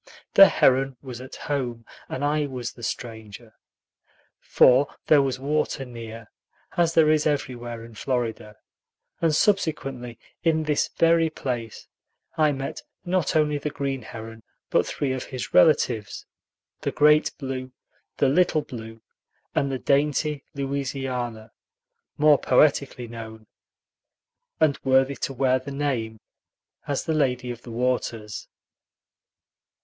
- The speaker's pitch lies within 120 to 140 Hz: Yes, low, 135 Hz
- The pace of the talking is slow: Yes, slow, 130 wpm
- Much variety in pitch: No, average, 3.6 semitones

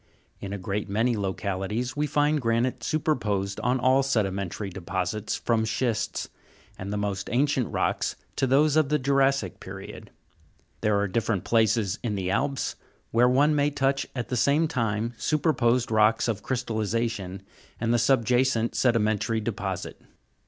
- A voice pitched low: Yes, low, 115 Hz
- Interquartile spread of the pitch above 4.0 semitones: Yes, average, 4.4 semitones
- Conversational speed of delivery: Yes, average, 145 wpm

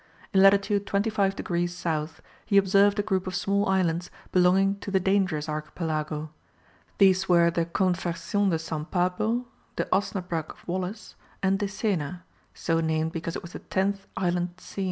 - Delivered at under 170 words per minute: Yes, average, 155 wpm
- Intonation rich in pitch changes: No, average, 2.8 semitones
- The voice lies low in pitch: No, medium, 185 Hz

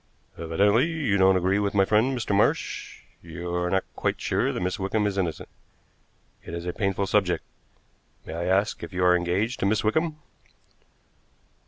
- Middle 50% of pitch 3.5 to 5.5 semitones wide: No, average, 3.0 semitones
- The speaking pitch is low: Yes, very low, 95 Hz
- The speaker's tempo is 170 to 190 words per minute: Yes, average, 175 wpm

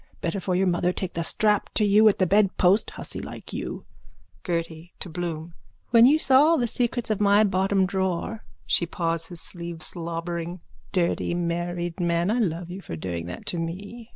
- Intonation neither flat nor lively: Yes, average, 3.3 semitones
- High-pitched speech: No, medium, 180 Hz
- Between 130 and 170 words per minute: No, average, 185 wpm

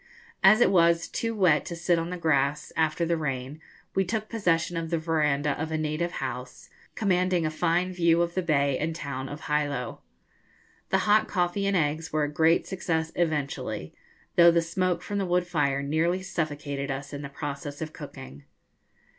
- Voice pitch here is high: No, medium, 160 Hz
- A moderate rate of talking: Yes, average, 185 wpm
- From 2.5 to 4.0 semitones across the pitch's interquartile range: Yes, average, 3.3 semitones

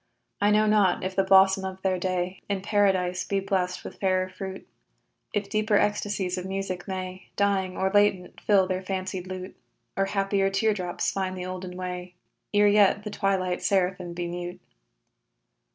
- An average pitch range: No, narrow, 1.4 semitones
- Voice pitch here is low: No, high, 190 Hz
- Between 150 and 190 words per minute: Yes, average, 170 wpm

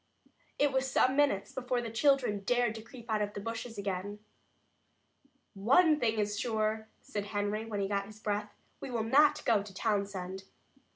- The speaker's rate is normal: Yes, average, 175 wpm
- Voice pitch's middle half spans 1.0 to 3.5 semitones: Yes, average, 3.1 semitones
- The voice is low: No, high, 220 Hz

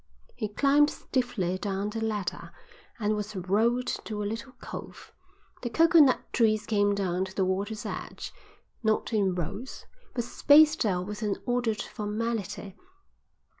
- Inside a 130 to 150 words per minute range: Yes, average, 140 wpm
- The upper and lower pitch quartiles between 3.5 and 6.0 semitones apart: No, average, 3.1 semitones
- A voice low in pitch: No, high, 215 Hz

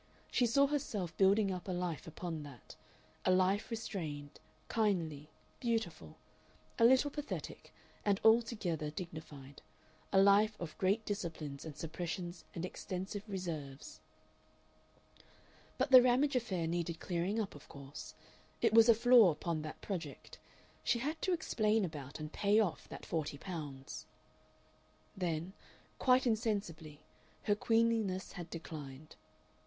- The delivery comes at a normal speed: No, slow, 130 wpm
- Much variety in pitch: Yes, wide, 5.8 semitones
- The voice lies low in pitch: No, medium, 185 Hz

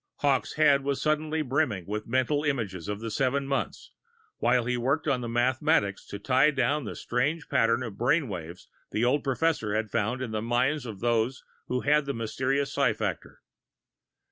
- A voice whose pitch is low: Yes, low, 125 Hz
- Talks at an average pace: Yes, average, 180 wpm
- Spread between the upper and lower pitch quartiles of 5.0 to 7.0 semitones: No, average, 3.7 semitones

